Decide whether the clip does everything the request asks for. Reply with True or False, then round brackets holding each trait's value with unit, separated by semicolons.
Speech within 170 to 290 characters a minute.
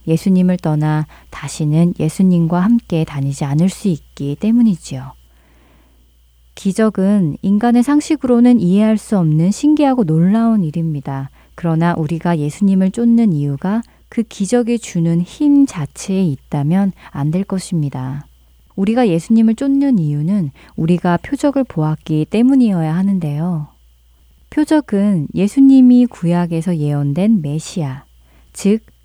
True (285 characters per minute)